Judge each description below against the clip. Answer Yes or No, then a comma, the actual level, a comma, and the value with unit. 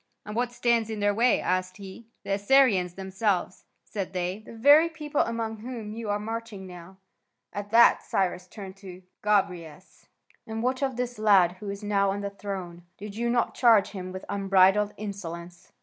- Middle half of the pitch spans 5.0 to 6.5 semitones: No, average, 3.3 semitones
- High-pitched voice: Yes, high, 205 Hz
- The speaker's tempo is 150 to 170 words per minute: No, average, 180 wpm